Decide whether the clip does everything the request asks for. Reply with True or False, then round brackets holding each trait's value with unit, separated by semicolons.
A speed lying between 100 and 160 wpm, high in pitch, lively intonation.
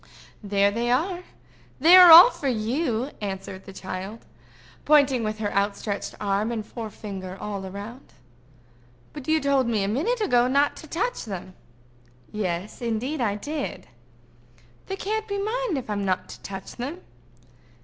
True (150 wpm; 235 Hz; 7.1 semitones)